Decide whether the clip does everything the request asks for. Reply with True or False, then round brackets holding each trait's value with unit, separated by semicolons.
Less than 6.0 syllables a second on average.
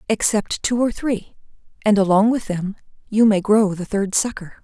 True (4.7 syllables/s)